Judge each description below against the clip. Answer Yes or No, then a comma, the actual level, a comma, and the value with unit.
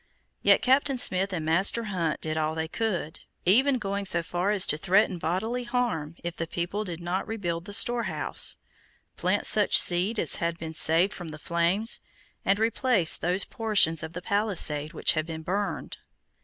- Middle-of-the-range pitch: Yes, medium, 180 Hz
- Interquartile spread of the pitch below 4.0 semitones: No, average, 4.3 semitones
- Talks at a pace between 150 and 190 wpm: Yes, average, 175 wpm